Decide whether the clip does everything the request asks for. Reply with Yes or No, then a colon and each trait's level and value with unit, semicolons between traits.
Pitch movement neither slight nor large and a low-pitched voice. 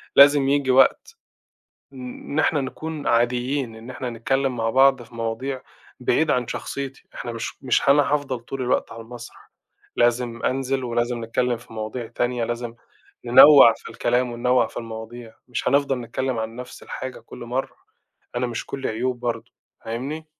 No: narrow, 2.3 semitones; low, 125 Hz